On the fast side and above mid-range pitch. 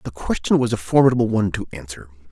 No: fast, 210 wpm; low, 100 Hz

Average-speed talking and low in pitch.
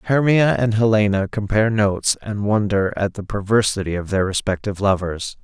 Yes: average, 155 wpm; low, 105 Hz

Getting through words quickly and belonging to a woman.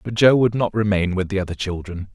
No: fast, 250 wpm; male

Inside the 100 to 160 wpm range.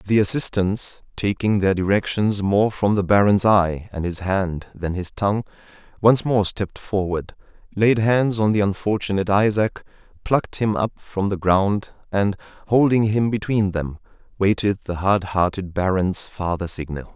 Yes: average, 155 wpm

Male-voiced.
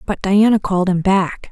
No: female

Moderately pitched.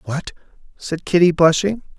Yes: medium, 170 Hz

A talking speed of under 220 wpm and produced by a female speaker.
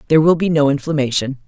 Yes: fast, 205 wpm; female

